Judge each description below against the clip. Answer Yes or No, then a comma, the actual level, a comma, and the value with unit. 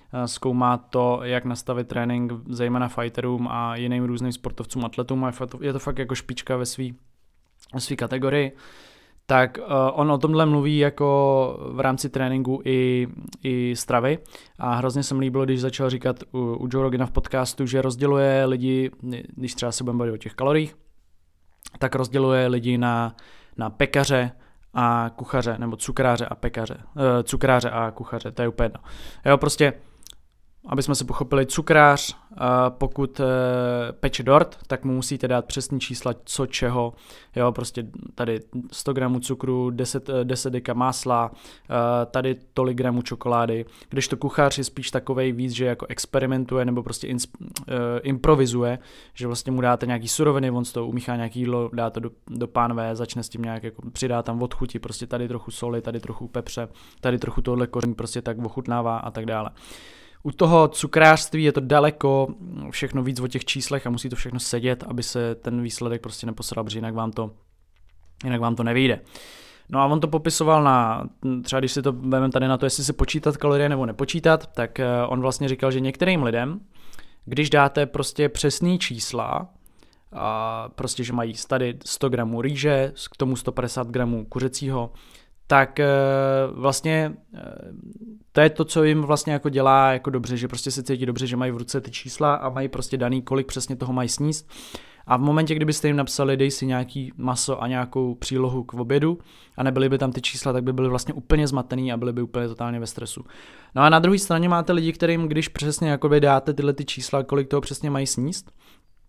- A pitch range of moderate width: No, narrow, 2.2 semitones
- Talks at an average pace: No, fast, 180 wpm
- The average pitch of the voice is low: Yes, low, 130 Hz